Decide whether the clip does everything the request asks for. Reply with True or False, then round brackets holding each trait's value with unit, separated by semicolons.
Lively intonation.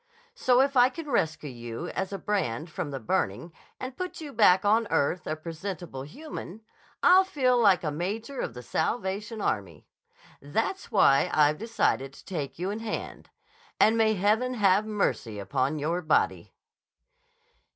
True (7.2 semitones)